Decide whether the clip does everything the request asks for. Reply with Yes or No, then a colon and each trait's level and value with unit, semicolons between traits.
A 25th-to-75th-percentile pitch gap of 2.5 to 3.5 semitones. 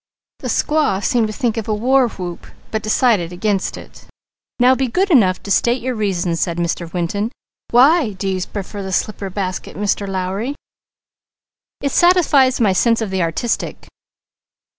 No: average, 4.8 semitones